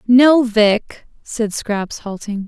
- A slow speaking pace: Yes, slow, 120 wpm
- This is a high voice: Yes, high, 220 Hz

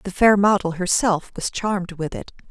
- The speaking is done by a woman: Yes, female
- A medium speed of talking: Yes, average, 190 wpm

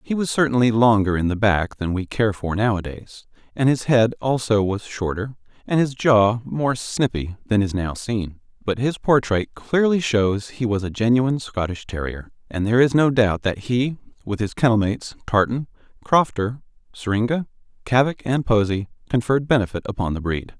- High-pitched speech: No, low, 115 Hz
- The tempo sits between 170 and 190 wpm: Yes, average, 175 wpm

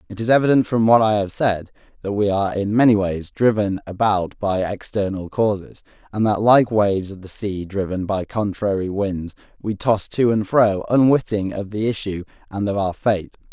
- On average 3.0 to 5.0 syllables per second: Yes, 4.9 syllables/s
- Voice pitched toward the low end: Yes, low, 105 Hz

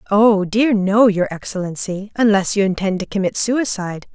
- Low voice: No, high, 200 Hz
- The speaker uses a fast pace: No, average, 160 wpm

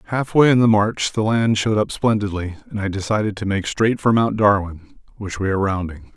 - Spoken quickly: Yes, fast, 225 wpm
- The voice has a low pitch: Yes, low, 105 Hz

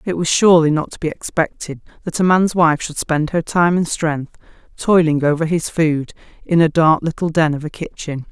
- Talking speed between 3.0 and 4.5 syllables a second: No, 5.1 syllables/s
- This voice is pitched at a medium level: Yes, medium, 160 Hz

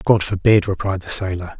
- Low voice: Yes, very low, 95 Hz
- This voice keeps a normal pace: Yes, average, 190 wpm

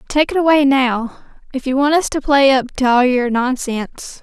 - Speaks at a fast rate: Yes, fast, 215 wpm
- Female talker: Yes, female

